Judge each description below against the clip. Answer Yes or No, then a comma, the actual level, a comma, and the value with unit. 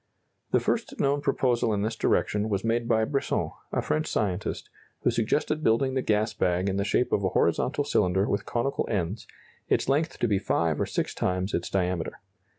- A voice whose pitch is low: Yes, low, 110 Hz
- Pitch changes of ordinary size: Yes, average, 4.3 semitones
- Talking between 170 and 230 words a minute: Yes, average, 190 wpm